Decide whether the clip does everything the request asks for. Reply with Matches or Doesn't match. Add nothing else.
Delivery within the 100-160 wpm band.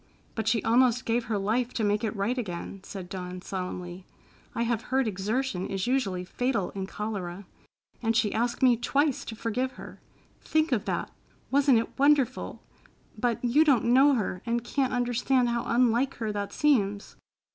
Doesn't match